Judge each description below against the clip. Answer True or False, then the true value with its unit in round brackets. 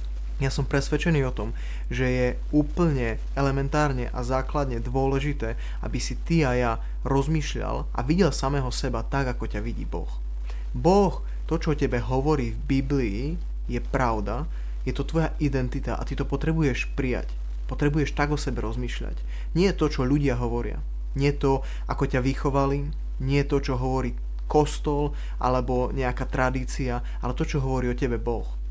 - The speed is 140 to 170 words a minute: True (160 wpm)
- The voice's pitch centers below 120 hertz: False (135 Hz)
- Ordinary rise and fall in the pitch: True (3.0 semitones)